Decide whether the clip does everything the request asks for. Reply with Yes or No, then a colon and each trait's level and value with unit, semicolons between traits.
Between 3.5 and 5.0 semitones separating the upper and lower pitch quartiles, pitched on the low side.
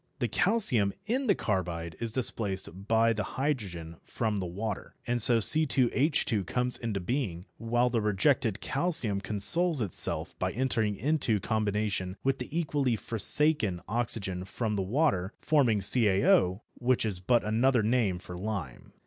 Yes: average, 4.7 semitones; low, 110 Hz